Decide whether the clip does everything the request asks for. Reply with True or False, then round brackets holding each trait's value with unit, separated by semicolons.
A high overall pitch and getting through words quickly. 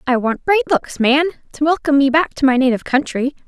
True (285 Hz; 225 wpm)